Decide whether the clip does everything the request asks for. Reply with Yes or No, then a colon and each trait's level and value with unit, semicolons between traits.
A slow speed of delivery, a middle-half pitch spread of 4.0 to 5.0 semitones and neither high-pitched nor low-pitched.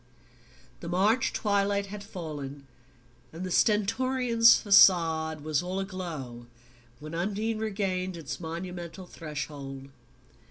Yes: slow, 105 wpm; average, 4.3 semitones; medium, 180 Hz